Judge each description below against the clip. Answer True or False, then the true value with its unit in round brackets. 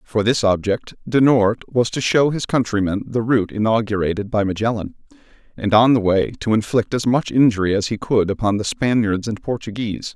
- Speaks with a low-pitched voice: True (110 Hz)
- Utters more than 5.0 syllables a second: True (5.4 syllables/s)